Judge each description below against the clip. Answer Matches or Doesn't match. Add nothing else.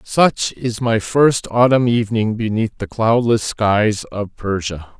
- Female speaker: Doesn't match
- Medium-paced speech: Matches